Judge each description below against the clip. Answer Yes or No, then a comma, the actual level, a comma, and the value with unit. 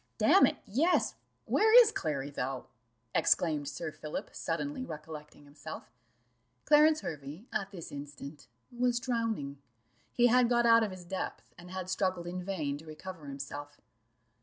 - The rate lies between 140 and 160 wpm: Yes, average, 145 wpm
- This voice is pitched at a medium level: Yes, medium, 175 Hz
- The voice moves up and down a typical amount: No, wide, 8.1 semitones